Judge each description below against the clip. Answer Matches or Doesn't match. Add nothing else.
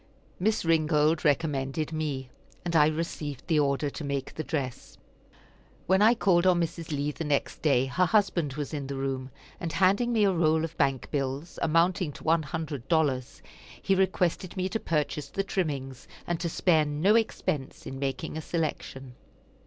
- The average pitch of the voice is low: Doesn't match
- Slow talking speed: Doesn't match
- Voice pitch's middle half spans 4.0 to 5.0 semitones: Doesn't match